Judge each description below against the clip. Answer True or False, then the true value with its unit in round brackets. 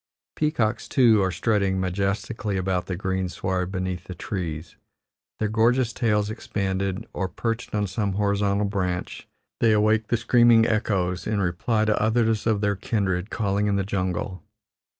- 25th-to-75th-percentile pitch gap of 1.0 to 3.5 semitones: True (2.8 semitones)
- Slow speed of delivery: False (150 wpm)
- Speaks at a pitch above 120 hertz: False (100 Hz)